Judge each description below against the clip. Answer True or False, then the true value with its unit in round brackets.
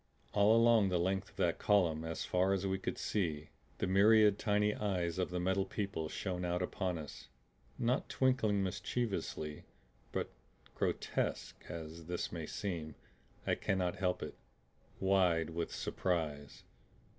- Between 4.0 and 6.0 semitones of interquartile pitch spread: False (3.2 semitones)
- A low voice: True (95 Hz)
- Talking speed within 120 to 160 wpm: True (145 wpm)